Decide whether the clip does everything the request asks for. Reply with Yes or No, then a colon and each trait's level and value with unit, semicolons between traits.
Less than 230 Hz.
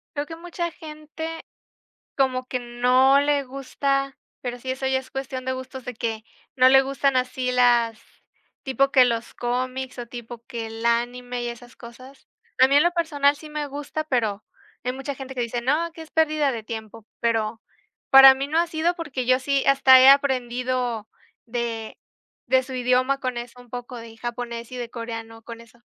No: very high, 255 Hz